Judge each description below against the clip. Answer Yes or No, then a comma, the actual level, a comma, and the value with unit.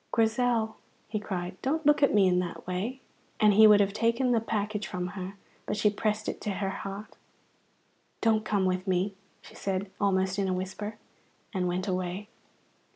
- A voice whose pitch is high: Yes, high, 205 Hz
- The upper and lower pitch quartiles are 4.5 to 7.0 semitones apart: No, narrow, 2.6 semitones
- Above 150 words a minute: Yes, average, 180 wpm